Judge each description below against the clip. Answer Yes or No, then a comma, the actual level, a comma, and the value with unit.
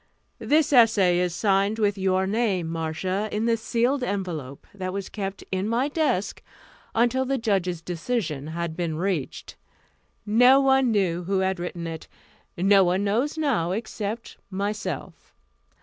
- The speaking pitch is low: No, high, 195 Hz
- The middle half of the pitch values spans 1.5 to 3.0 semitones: No, average, 4.4 semitones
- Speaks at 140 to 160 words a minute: Yes, average, 145 wpm